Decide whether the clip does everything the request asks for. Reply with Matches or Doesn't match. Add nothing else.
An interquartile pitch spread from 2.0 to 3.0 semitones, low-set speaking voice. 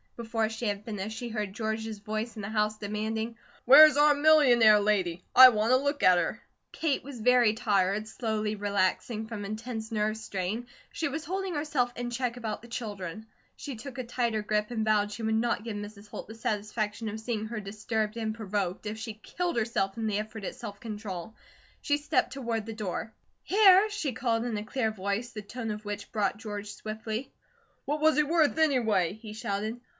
Doesn't match